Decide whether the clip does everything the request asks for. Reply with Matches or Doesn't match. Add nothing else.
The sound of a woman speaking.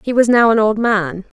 Matches